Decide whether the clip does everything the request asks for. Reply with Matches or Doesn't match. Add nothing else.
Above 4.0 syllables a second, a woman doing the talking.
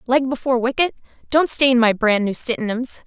Matches